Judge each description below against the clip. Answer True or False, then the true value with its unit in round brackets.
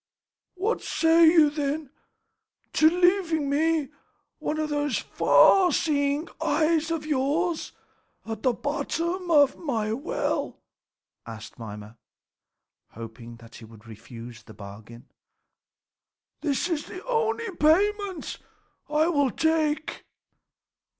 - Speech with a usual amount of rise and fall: False (6.9 semitones)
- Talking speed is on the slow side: True (105 wpm)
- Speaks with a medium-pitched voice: False (300 Hz)